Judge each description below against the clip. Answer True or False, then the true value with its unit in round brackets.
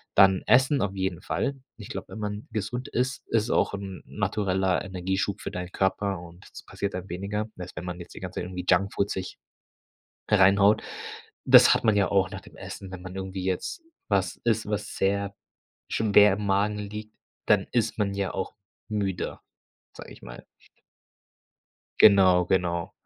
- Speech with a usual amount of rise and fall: False (2.1 semitones)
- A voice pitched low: True (100 Hz)